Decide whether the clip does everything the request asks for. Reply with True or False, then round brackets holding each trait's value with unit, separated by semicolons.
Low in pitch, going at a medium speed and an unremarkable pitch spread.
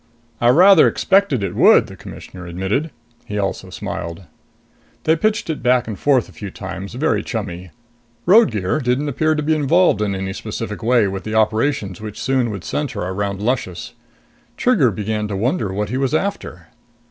False (110 Hz; 170 wpm; 6.9 semitones)